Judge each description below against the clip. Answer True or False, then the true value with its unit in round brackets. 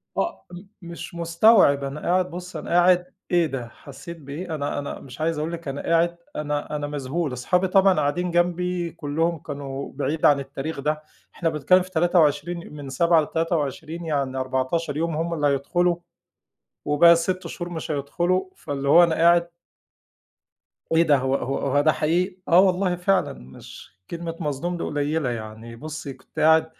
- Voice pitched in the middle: True (160 Hz)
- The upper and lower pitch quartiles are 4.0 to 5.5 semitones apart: False (3.3 semitones)